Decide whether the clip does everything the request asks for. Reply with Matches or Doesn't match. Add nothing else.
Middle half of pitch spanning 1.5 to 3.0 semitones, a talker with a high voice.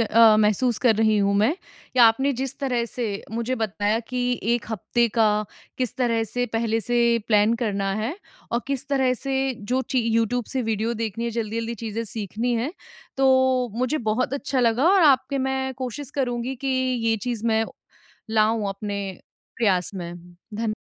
Matches